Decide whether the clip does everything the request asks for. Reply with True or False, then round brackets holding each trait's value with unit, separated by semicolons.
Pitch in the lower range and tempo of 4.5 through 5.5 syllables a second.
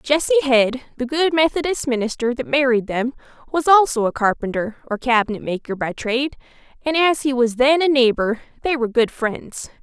False (255 Hz; 5.3 syllables/s)